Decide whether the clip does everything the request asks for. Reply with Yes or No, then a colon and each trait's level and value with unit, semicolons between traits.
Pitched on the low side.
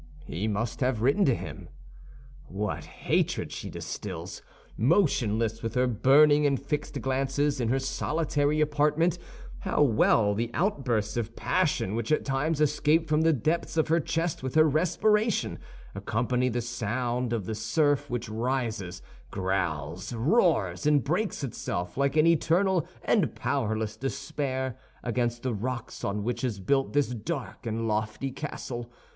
Yes: low, 130 Hz